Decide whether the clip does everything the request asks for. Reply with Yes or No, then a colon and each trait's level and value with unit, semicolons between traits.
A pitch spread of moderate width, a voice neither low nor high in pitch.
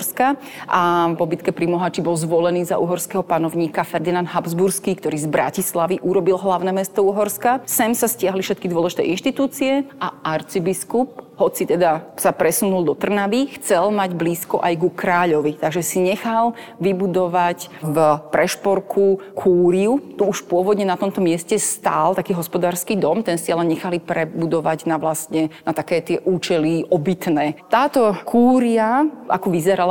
Yes: average, 3.0 semitones; medium, 180 Hz